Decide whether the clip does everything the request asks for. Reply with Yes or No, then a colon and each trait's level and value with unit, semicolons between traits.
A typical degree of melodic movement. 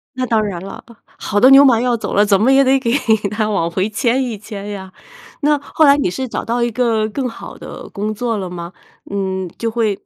Yes: average, 4.0 semitones